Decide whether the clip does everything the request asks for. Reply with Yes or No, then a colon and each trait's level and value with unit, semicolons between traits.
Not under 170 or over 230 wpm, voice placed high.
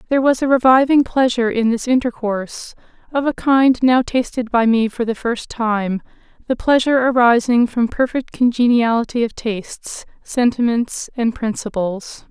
No: average, 140 wpm; high, 240 Hz